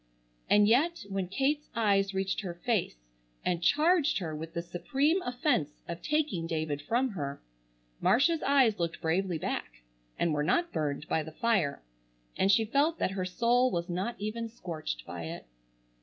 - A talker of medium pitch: No, high, 195 Hz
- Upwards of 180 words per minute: No, average, 165 wpm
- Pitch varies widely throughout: Yes, wide, 7.1 semitones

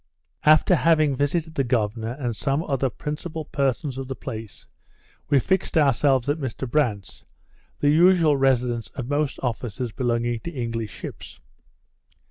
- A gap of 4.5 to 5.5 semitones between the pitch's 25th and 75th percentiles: No, average, 4.0 semitones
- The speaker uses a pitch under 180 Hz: Yes, low, 135 Hz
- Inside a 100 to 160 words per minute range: Yes, average, 140 wpm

